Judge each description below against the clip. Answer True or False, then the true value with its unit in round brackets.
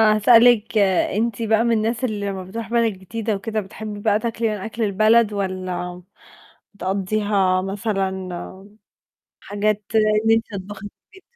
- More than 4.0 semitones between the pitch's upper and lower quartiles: False (2.6 semitones)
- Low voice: False (210 Hz)